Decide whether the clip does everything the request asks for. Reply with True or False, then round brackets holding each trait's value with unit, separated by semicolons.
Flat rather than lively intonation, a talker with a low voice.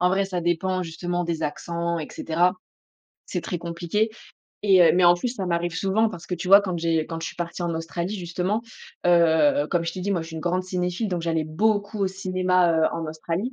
False (2.1 semitones; 175 Hz)